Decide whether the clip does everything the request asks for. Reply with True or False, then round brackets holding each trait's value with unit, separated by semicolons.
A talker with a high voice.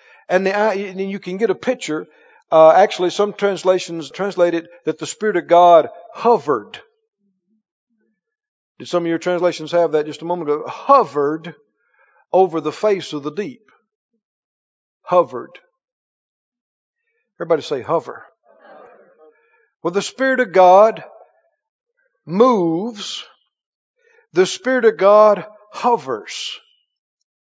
True (200 Hz)